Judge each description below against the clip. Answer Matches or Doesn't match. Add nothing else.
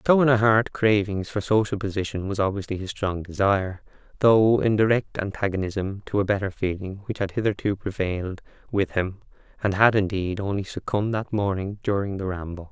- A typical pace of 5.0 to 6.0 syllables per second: Matches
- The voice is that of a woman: Doesn't match